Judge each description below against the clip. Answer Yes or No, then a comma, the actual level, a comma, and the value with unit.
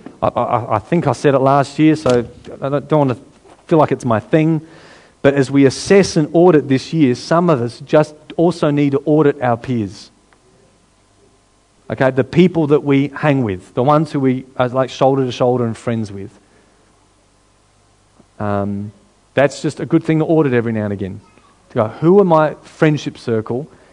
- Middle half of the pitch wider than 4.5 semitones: Yes, wide, 5.4 semitones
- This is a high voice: No, low, 135 Hz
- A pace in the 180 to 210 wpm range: Yes, average, 190 wpm